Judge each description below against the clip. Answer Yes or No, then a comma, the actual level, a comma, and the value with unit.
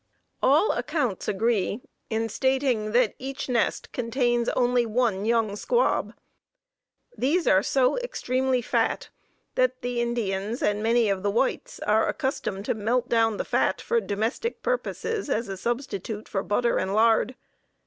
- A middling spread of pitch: Yes, average, 3.3 semitones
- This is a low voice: No, high, 235 Hz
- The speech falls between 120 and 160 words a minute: Yes, average, 145 wpm